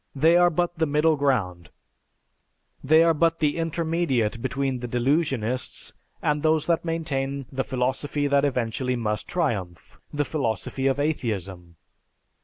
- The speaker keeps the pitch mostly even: No, average, 4.5 semitones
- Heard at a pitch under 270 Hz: Yes, medium, 140 Hz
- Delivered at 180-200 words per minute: No, slow, 135 wpm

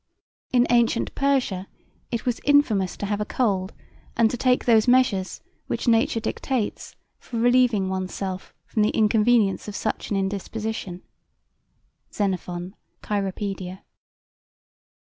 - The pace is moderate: No, slow, 125 wpm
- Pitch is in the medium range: No, high, 215 Hz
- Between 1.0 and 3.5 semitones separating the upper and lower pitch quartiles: No, average, 3.9 semitones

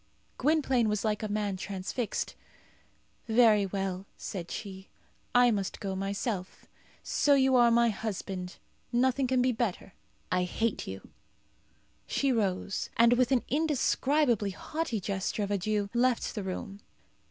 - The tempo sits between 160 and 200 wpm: No, slow, 135 wpm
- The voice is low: No, high, 215 Hz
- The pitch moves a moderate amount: Yes, average, 4.1 semitones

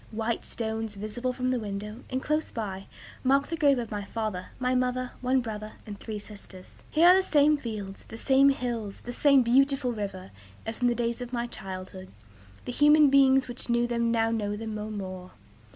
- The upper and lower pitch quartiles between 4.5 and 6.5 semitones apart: No, average, 3.5 semitones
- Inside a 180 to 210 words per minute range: Yes, average, 200 wpm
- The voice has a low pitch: No, high, 235 Hz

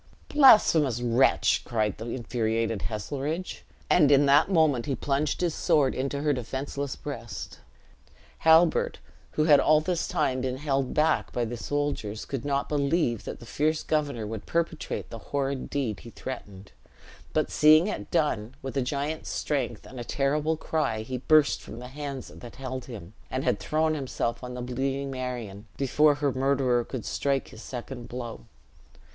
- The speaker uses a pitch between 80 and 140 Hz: Yes, low, 135 Hz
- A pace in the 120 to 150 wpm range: No, average, 165 wpm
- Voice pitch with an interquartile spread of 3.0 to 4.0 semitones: Yes, average, 3.7 semitones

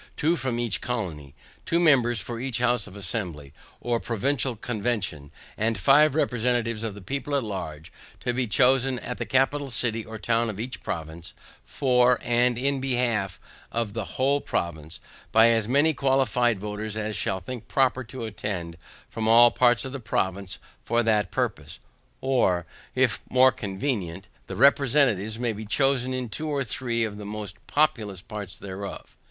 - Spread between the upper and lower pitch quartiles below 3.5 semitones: No, average, 4.0 semitones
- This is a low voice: Yes, low, 115 Hz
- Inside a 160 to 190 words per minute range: Yes, average, 165 wpm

